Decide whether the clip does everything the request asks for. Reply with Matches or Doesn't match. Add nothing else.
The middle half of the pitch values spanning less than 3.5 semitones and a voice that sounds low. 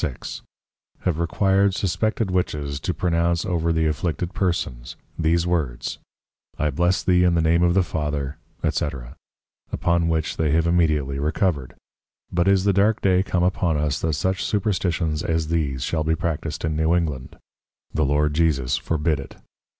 Matches